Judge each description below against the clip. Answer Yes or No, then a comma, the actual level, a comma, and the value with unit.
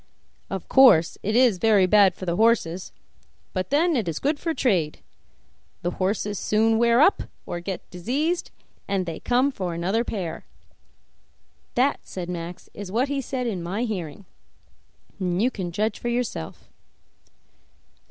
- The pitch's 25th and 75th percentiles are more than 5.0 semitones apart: Yes, wide, 5.4 semitones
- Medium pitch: No, high, 205 Hz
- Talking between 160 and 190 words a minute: No, average, 150 wpm